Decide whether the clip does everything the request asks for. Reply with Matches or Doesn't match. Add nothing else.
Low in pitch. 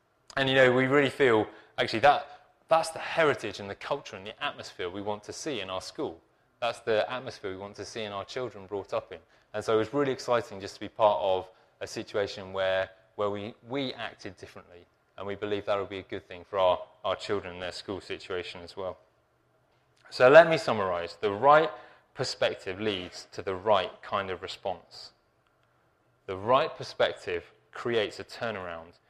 Matches